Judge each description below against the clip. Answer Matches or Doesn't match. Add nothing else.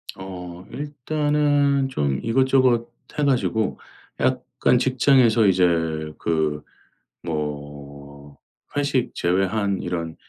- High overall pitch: Doesn't match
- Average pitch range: Doesn't match